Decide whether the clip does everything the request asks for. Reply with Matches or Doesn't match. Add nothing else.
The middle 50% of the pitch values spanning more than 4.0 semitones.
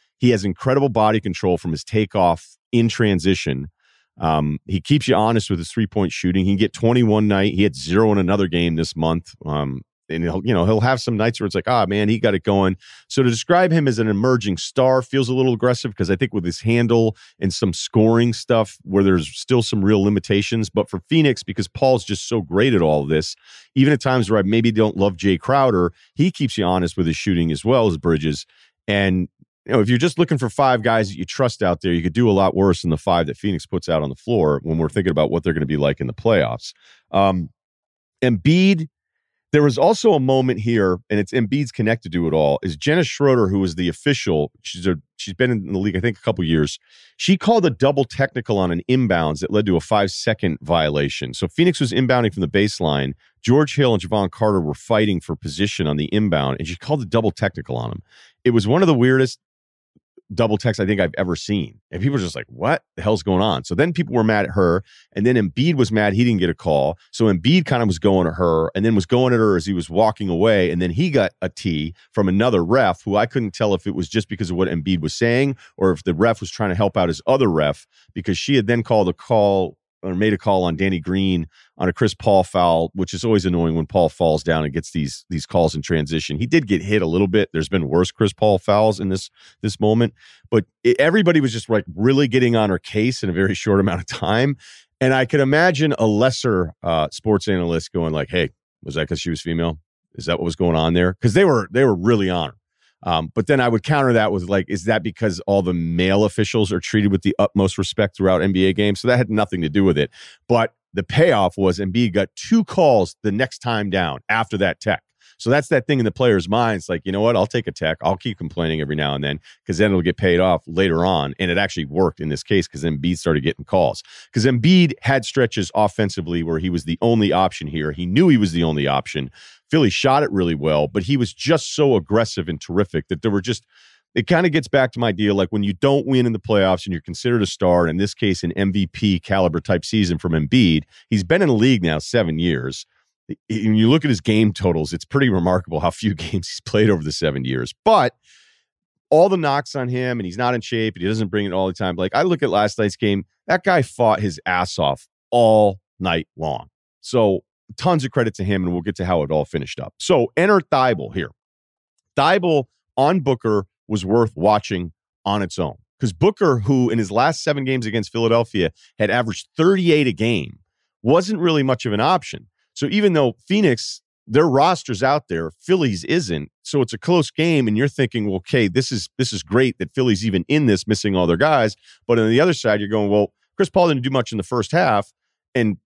Matches